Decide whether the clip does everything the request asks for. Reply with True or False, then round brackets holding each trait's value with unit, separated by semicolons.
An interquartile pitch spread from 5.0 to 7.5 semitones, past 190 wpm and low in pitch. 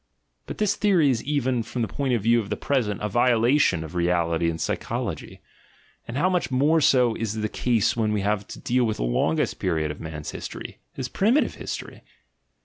True (5.3 semitones; 200 wpm; 115 Hz)